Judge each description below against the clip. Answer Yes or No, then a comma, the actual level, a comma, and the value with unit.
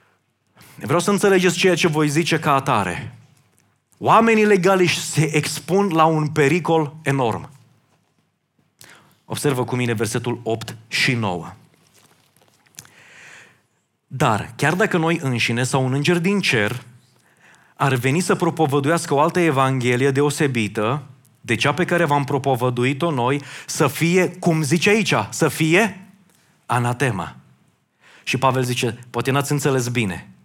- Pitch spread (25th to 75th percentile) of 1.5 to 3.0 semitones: No, average, 5.2 semitones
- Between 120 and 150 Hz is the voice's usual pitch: Yes, medium, 140 Hz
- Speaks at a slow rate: No, average, 125 wpm